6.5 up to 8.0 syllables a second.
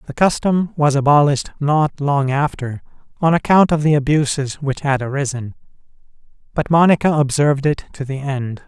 No: 5.2 syllables/s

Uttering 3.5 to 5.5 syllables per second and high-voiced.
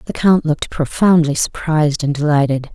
No: 5.4 syllables/s; medium, 155 Hz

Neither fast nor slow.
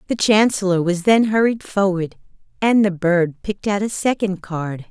Yes: average, 170 wpm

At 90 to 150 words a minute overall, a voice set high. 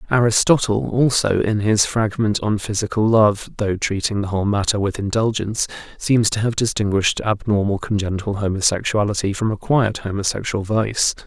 No: average, 140 wpm; low, 105 Hz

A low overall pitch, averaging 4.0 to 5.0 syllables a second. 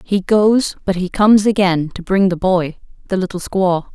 No: high, 190 Hz; 4.7 syllables/s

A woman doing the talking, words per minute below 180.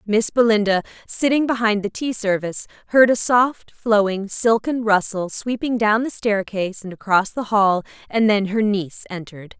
Yes: female; average, 165 wpm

